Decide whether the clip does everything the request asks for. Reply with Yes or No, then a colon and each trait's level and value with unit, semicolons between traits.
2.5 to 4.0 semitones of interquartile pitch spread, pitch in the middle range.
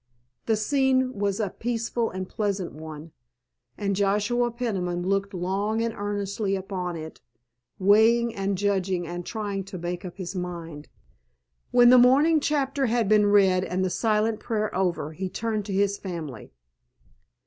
No: average, 3.6 semitones; high, 200 Hz